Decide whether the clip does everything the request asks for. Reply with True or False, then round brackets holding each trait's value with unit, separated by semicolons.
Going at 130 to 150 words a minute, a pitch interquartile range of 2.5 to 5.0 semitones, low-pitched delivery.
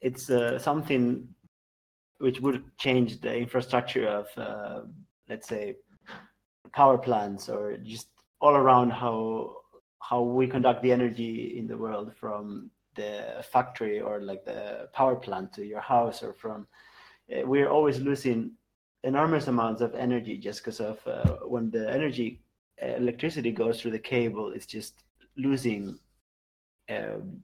True (140 wpm; 2.8 semitones; 120 Hz)